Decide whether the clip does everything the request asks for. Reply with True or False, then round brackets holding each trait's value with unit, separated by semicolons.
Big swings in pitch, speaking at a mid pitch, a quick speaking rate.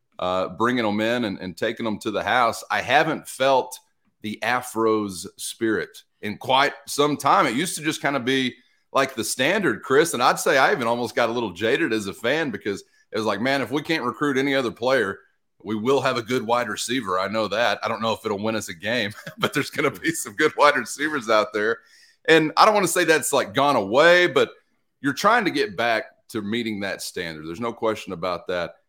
False (5.9 semitones; 120 Hz; 235 wpm)